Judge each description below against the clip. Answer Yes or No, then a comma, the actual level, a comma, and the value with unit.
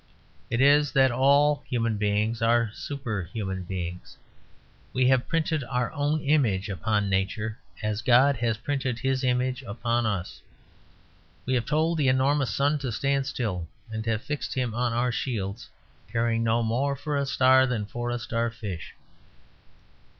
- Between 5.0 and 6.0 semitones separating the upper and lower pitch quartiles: No, average, 3.6 semitones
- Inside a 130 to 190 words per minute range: Yes, average, 150 wpm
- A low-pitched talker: Yes, low, 120 Hz